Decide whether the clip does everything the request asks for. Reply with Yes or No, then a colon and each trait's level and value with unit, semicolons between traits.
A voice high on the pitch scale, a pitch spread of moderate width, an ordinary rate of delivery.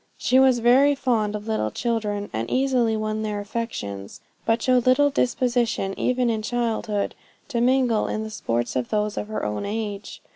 Yes: high, 225 Hz; average, 3.0 semitones; average, 175 wpm